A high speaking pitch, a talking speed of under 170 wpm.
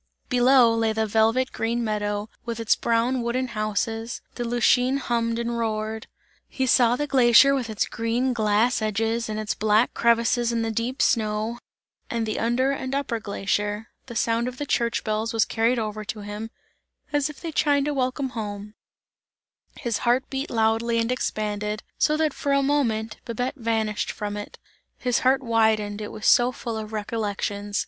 No: high, 230 Hz; average, 175 wpm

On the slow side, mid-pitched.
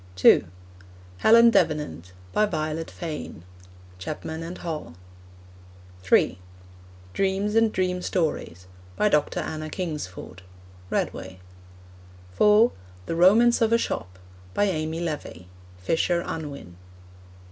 Yes: slow, 105 wpm; medium, 160 Hz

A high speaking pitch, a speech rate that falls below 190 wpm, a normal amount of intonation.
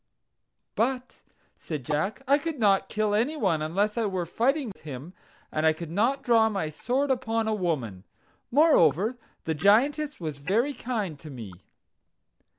No: high, 210 Hz; average, 155 wpm; wide, 7.8 semitones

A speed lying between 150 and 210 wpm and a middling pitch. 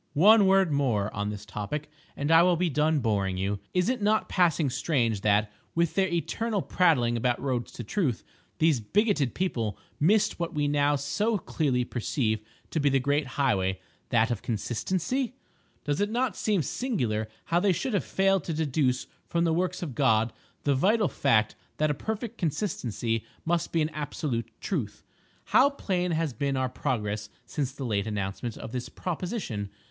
Yes: average, 175 wpm; medium, 145 Hz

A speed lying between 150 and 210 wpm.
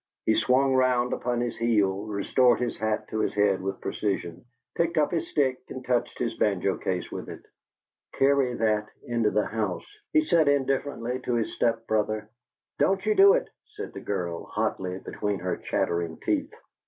Yes: average, 175 wpm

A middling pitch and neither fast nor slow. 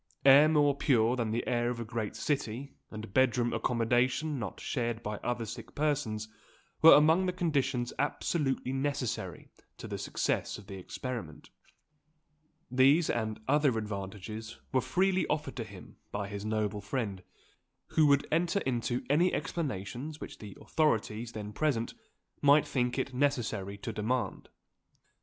No: low, 125 Hz; average, 145 wpm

